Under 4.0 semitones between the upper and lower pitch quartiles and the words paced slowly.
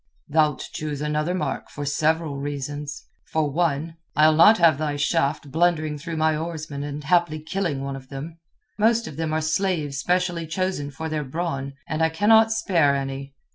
No: average, 2.7 semitones; average, 175 wpm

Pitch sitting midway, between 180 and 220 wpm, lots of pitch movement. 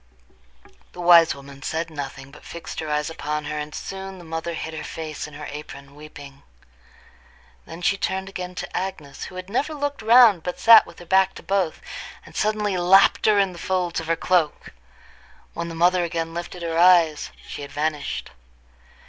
No: medium, 170 Hz; average, 190 wpm; average, 3.7 semitones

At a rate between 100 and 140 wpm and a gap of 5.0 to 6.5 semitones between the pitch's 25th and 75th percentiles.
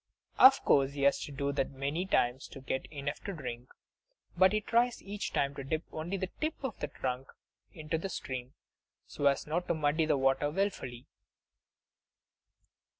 No: average, 175 wpm; wide, 5.6 semitones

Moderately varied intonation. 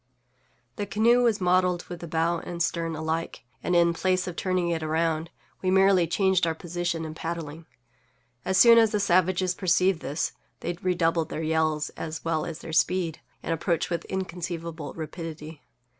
No: narrow, 2.2 semitones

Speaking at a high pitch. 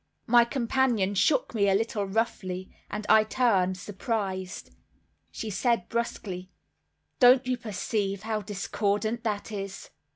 Yes: high, 215 Hz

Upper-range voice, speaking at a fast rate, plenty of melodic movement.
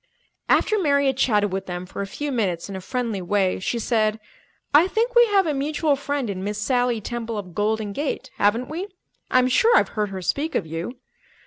Yes: high, 235 Hz; fast, 210 wpm; wide, 6.1 semitones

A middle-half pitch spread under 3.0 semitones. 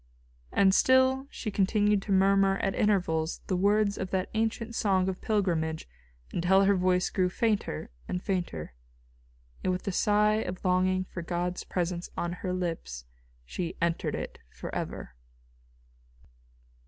Yes: narrow, 2.4 semitones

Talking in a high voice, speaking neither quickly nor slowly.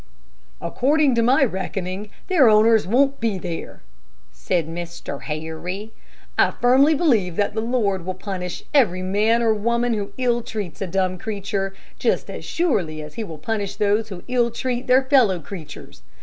Yes: high, 210 Hz; average, 165 wpm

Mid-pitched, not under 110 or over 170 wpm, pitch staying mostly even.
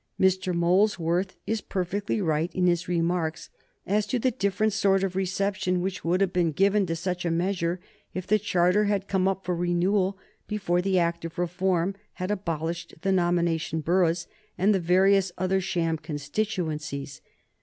Yes: medium, 180 Hz; average, 165 wpm; narrow, 2.3 semitones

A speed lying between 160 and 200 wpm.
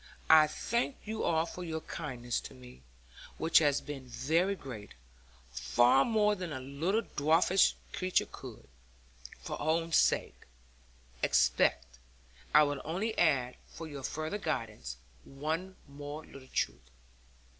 No: slow, 135 wpm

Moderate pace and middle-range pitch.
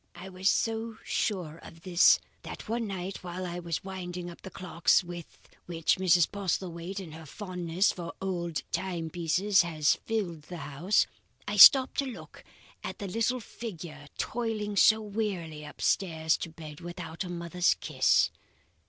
Yes: average, 155 wpm; medium, 180 Hz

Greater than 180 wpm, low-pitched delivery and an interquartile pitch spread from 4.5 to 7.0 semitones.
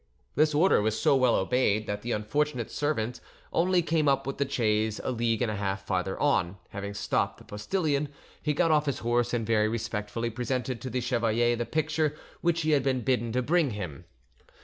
Yes: average, 200 wpm; low, 120 Hz; average, 5.2 semitones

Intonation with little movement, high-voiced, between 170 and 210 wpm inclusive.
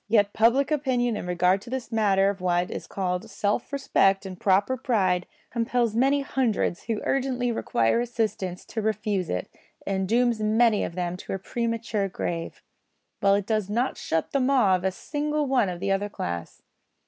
No: average, 4.2 semitones; high, 210 Hz; average, 180 wpm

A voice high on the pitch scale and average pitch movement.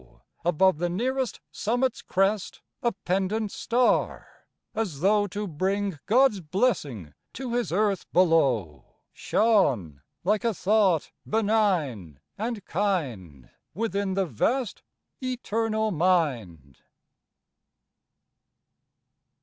No: high, 195 Hz; wide, 6.1 semitones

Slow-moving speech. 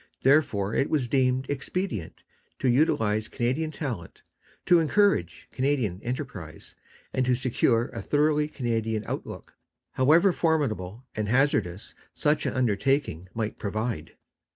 Yes: slow, 120 wpm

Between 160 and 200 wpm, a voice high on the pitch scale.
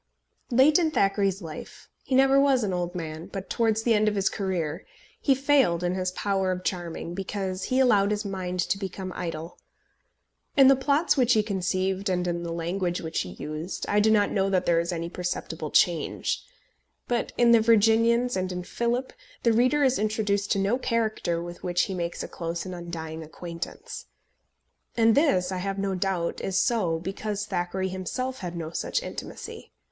Yes: average, 185 wpm; high, 195 Hz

